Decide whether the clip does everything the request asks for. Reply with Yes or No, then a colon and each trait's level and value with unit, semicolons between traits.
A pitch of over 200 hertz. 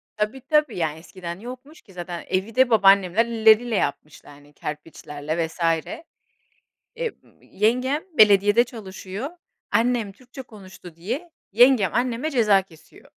Yes: high, 210 Hz